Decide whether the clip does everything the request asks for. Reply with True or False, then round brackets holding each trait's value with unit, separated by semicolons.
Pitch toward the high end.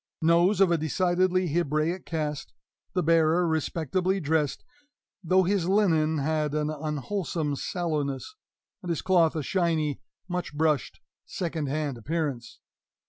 False (160 Hz)